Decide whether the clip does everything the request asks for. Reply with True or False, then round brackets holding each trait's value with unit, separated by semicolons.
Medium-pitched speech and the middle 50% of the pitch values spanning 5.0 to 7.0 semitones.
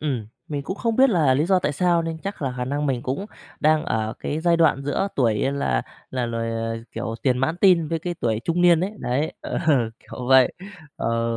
True (145 Hz; 5.4 semitones)